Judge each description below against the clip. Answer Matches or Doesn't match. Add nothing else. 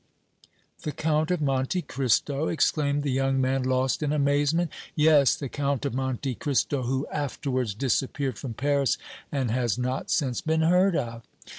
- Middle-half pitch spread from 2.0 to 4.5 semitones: Matches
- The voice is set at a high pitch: Doesn't match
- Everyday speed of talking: Matches